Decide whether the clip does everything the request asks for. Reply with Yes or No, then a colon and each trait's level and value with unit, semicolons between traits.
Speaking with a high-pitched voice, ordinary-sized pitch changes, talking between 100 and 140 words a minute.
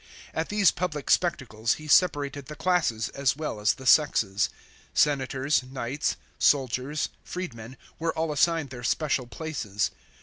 No: medium, 140 Hz; average, 4.2 semitones; slow, 135 wpm